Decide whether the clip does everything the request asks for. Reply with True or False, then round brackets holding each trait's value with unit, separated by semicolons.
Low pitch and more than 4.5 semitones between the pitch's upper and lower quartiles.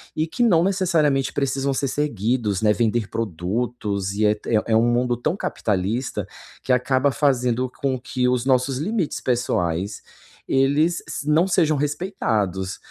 True (125 Hz; 4.9 semitones)